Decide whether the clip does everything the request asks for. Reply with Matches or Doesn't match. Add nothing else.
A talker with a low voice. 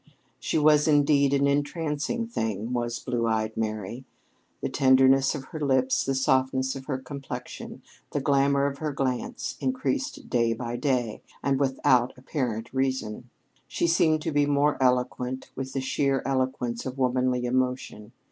Matches